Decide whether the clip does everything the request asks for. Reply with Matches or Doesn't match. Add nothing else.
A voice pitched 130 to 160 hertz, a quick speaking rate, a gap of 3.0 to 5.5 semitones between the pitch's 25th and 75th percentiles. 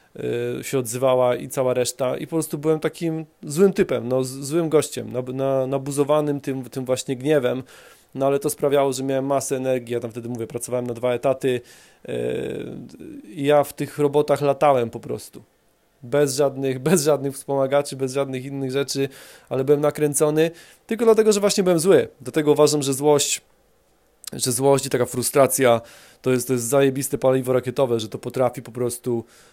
Doesn't match